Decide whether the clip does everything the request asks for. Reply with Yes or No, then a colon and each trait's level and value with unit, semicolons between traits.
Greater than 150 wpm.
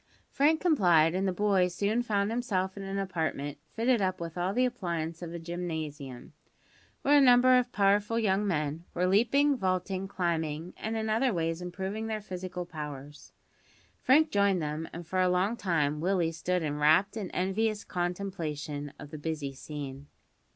Yes: average, 170 wpm